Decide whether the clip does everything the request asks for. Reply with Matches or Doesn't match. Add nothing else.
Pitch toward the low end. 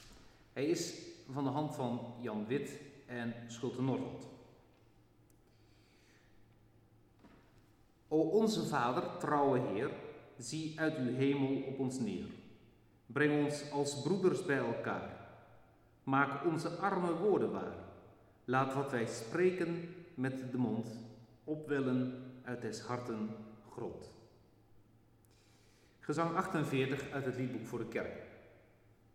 Matches